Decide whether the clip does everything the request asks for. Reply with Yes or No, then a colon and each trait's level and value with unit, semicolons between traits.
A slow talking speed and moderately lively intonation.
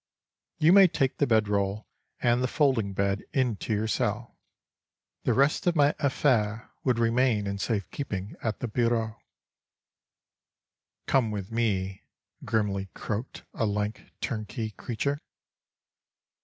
Yes: slow, 125 wpm; average, 3.7 semitones